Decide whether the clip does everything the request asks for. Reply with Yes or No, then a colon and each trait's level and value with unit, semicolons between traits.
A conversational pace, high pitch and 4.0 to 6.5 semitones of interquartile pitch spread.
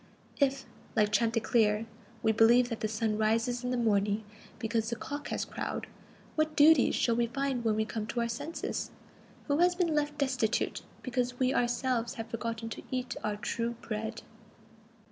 No: average, 170 wpm; high, 235 Hz; average, 2.7 semitones